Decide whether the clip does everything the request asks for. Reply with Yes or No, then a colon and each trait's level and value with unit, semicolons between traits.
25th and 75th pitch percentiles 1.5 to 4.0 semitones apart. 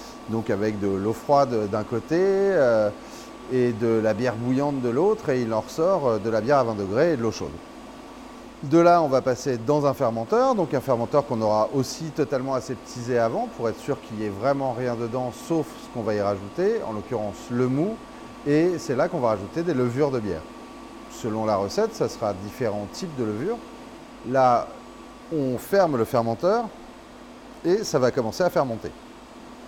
No: average, 4.4 semitones